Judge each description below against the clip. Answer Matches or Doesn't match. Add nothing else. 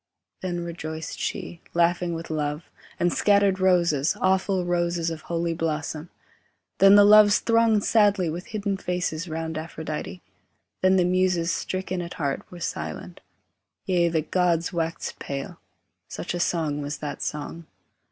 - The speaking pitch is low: Doesn't match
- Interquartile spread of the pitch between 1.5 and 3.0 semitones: Matches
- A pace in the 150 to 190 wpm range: Doesn't match